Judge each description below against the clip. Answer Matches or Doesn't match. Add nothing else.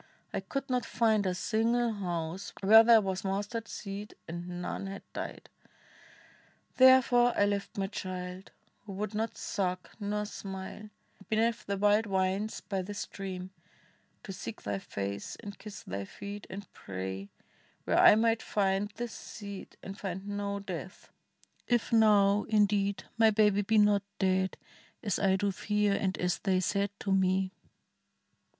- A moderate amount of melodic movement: Doesn't match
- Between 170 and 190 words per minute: Doesn't match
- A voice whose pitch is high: Matches